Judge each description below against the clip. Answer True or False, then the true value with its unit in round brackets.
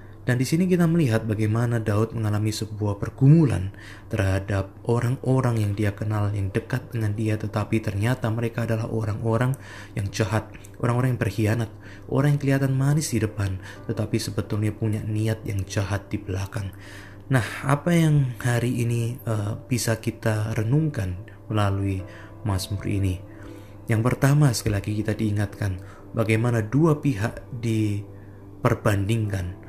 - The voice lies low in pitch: True (110 Hz)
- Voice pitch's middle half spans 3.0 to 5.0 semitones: False (2.6 semitones)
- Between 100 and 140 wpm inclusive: True (135 wpm)